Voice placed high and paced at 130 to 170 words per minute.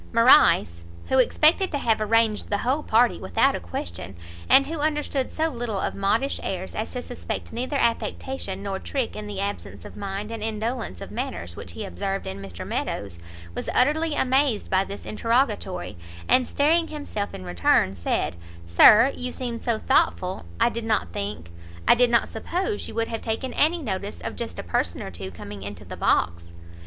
No: high, 220 Hz; average, 185 wpm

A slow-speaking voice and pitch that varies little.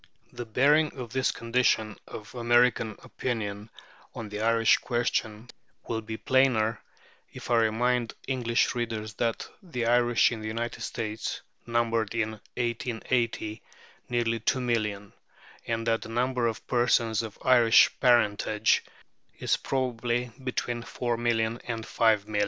Yes: slow, 125 wpm; narrow, 1.7 semitones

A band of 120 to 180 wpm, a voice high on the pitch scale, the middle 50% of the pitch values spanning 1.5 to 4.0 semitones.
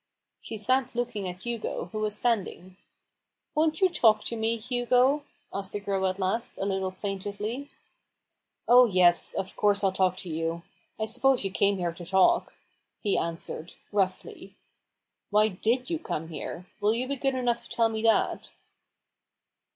No: average, 165 wpm; high, 210 Hz; average, 4.4 semitones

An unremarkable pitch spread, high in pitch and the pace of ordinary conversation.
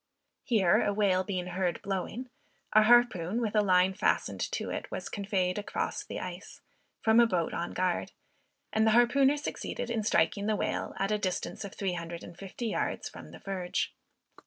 Yes: average, 3.3 semitones; high, 200 Hz; average, 185 wpm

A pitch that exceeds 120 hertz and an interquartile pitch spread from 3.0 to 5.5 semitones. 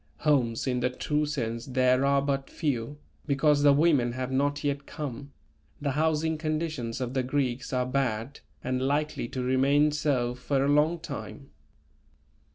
No: medium, 140 Hz; narrow, 2.6 semitones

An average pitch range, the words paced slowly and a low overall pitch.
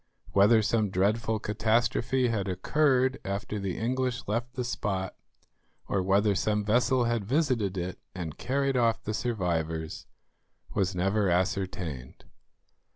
Yes: average, 4.1 semitones; slow, 125 wpm; low, 105 Hz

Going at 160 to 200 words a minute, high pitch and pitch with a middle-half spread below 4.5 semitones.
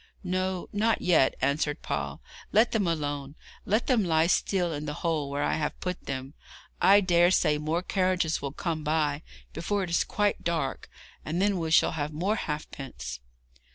No: average, 175 wpm; medium, 165 Hz; average, 4.0 semitones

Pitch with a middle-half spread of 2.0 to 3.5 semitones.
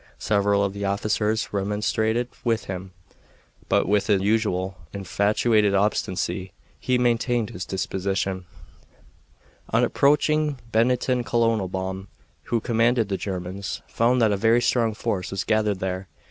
Yes: average, 3.0 semitones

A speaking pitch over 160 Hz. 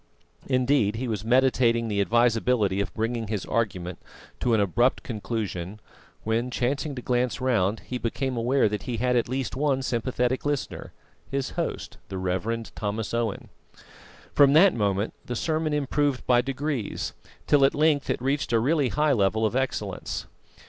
No: low, 120 Hz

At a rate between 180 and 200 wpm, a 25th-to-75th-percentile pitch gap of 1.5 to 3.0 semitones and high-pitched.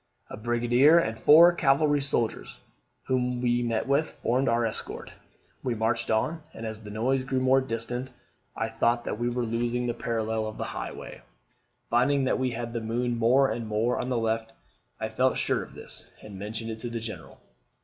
No: average, 190 wpm; narrow, 2.4 semitones; low, 120 Hz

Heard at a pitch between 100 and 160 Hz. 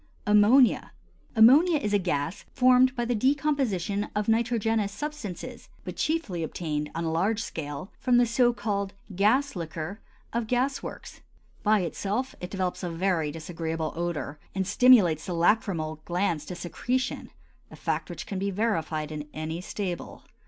No: high, 200 Hz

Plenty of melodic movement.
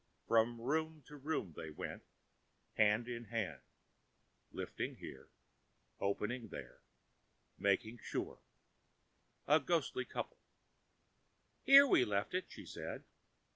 Yes: wide, 6.5 semitones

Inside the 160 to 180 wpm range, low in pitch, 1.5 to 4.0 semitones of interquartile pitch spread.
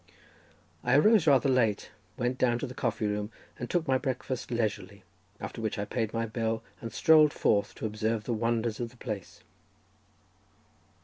Yes: average, 170 wpm; low, 115 Hz; average, 2.9 semitones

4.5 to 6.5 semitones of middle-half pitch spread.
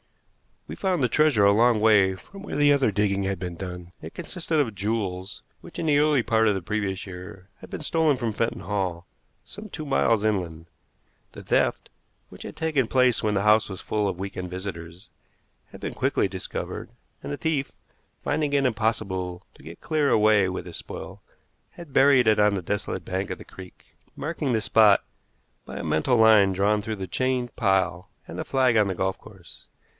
Yes: wide, 5.4 semitones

